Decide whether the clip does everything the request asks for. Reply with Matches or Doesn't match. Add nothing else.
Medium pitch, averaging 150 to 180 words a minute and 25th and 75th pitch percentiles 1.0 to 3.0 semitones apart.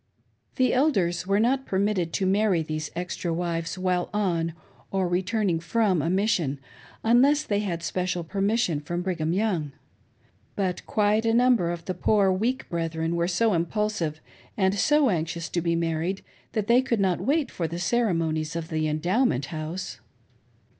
Doesn't match